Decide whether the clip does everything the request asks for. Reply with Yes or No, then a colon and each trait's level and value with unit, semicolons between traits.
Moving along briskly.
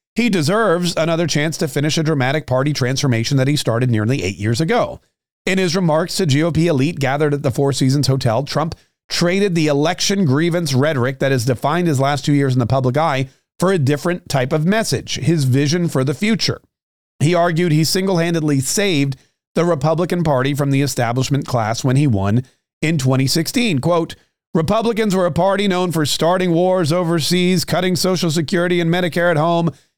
No: average, 185 wpm